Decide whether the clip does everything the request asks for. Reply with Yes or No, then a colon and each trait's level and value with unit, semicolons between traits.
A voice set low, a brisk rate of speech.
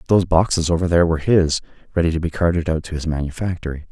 Yes: very low, 85 Hz; fast, 215 wpm